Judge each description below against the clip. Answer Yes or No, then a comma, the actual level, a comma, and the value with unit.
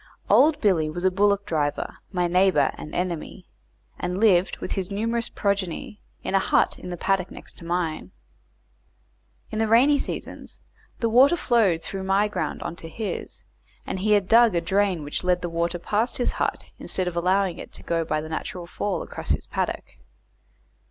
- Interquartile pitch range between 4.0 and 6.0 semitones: No, average, 3.3 semitones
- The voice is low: No, medium, 185 Hz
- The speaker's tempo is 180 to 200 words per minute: Yes, average, 185 wpm